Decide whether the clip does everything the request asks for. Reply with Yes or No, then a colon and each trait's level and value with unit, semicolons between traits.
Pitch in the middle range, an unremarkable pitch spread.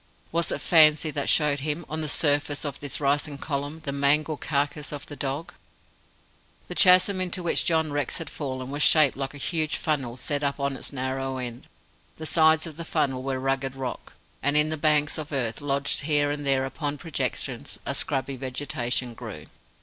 No: medium, 145 Hz; narrow, 2.3 semitones